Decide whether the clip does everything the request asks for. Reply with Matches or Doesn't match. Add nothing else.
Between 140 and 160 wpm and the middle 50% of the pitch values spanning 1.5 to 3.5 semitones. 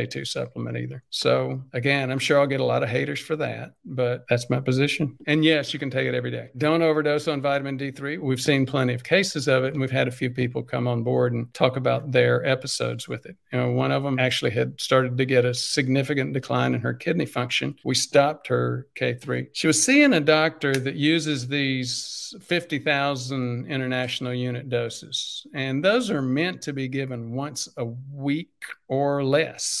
Doesn't match